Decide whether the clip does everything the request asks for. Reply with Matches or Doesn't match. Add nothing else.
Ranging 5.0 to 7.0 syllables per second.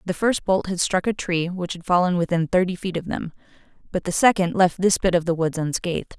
Matches